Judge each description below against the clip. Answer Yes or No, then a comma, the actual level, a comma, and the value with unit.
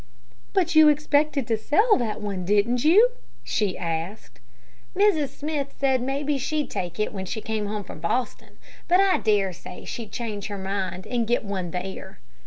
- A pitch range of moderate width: No, wide, 6.9 semitones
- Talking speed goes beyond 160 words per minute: Yes, average, 175 wpm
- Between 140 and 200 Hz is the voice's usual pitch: No, high, 225 Hz